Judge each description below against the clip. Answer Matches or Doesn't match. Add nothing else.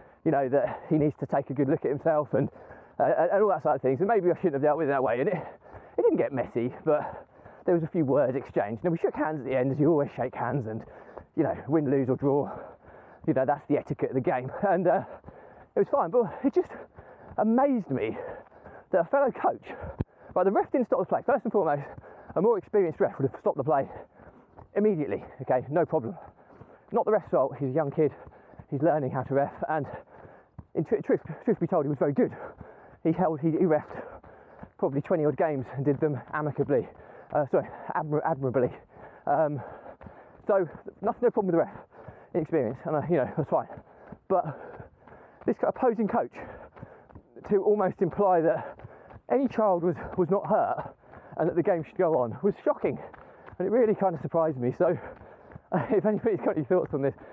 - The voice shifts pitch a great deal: Matches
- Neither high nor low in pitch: Matches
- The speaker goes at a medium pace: Doesn't match